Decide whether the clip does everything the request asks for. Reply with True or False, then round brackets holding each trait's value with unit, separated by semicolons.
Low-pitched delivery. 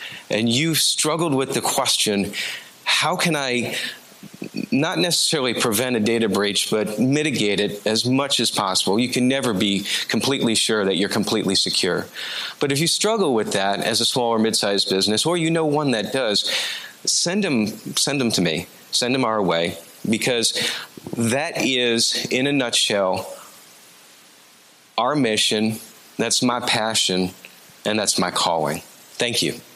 True (115 Hz)